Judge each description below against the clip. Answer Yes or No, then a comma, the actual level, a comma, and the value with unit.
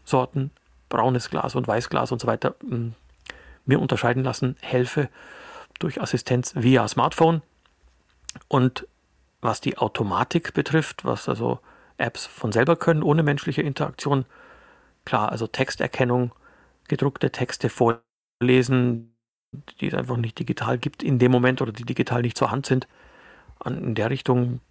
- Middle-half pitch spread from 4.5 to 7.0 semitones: No, average, 2.8 semitones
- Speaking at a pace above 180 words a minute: No, average, 140 wpm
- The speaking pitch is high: No, low, 125 Hz